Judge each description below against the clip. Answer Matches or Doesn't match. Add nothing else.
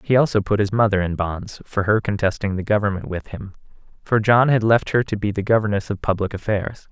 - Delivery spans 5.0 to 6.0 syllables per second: Matches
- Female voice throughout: Doesn't match